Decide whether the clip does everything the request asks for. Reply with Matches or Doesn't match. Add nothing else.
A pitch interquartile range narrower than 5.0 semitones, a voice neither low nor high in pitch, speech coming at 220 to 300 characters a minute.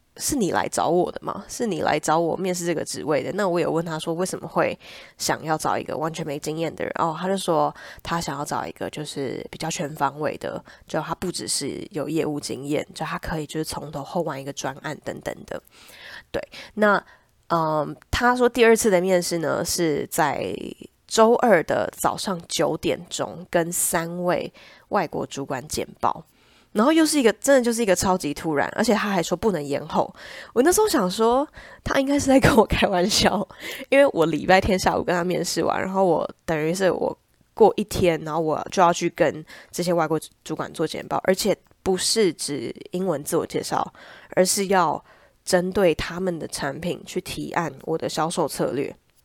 Matches